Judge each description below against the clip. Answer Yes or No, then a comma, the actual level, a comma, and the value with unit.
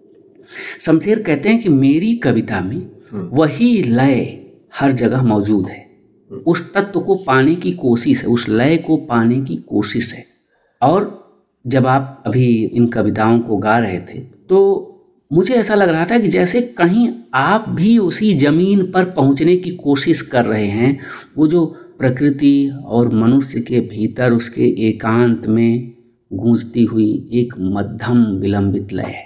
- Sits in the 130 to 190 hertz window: Yes, low, 135 Hz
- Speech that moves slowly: No, average, 150 wpm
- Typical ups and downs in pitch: No, wide, 7.0 semitones